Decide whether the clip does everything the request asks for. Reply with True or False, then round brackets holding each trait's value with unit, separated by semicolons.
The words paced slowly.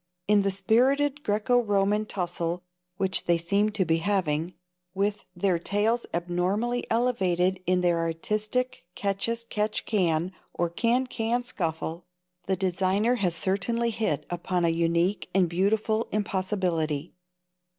True (130 wpm)